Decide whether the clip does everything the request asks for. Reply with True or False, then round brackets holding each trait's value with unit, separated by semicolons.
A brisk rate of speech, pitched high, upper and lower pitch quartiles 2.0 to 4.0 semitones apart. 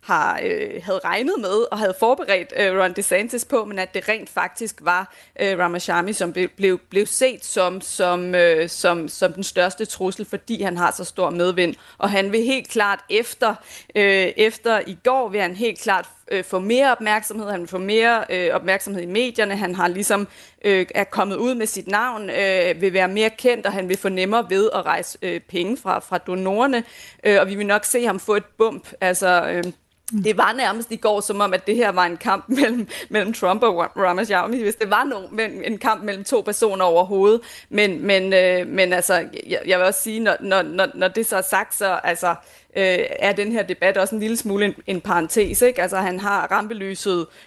False (210 wpm; 200 Hz; 2.9 semitones)